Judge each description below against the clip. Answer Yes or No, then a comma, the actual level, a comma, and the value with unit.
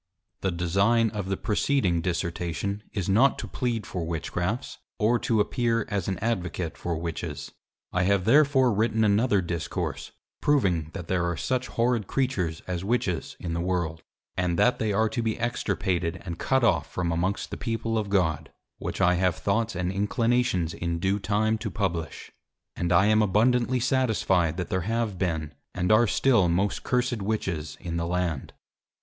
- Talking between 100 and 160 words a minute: No, average, 170 wpm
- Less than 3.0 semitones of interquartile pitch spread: No, average, 4.8 semitones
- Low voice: Yes, low, 100 Hz